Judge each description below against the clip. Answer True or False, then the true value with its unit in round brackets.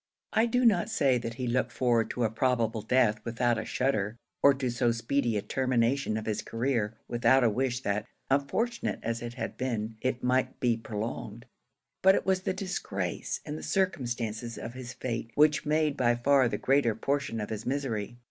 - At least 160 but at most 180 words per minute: False (190 wpm)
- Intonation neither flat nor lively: True (3.2 semitones)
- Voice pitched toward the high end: False (120 Hz)